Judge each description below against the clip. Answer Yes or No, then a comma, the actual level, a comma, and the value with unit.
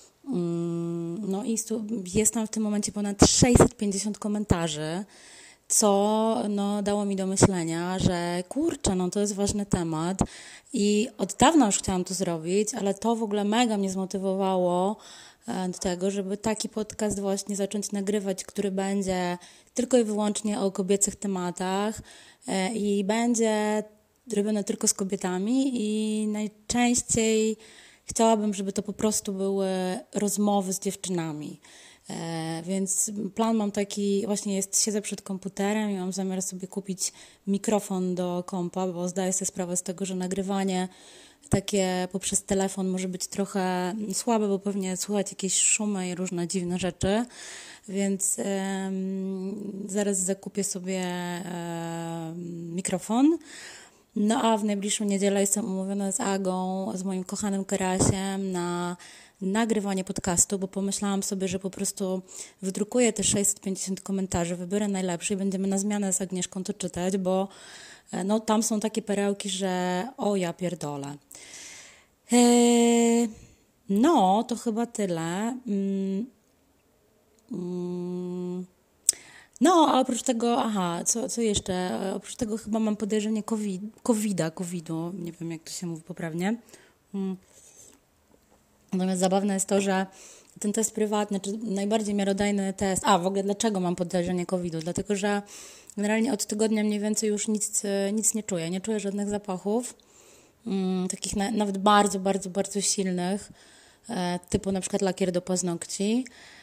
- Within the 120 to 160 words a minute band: Yes, average, 140 wpm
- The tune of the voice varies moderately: No, narrow, 2.2 semitones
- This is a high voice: Yes, high, 195 Hz